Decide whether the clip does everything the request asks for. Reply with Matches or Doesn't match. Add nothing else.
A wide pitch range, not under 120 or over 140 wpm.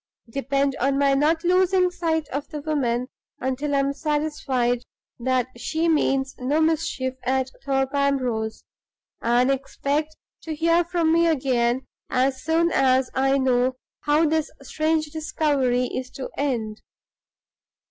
Doesn't match